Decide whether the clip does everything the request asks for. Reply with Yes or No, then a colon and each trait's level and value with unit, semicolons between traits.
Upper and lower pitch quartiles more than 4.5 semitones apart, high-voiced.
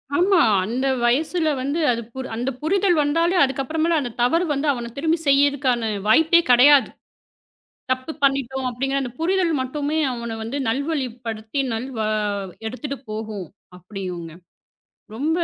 Yes: average, 5.0 semitones; very high, 270 Hz